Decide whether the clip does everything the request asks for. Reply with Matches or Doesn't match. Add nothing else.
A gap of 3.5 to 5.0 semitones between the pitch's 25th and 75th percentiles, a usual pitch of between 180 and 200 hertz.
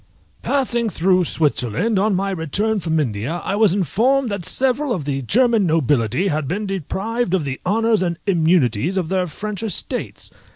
Doesn't match